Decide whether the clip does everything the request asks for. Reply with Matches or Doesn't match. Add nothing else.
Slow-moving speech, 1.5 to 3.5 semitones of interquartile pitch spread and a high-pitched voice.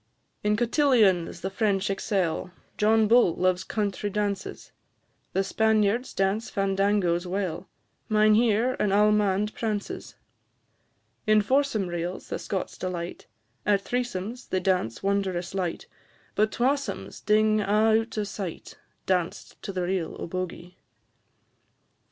Matches